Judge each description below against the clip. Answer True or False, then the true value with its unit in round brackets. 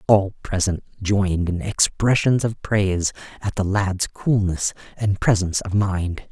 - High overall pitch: False (100 Hz)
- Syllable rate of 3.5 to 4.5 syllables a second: True (4.3 syllables/s)